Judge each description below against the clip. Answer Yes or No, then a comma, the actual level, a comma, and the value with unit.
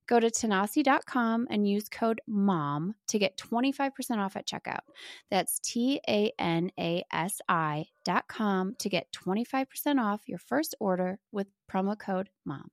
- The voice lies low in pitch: No, high, 205 Hz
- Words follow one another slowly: Yes, slow, 125 wpm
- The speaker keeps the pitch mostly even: No, average, 4.2 semitones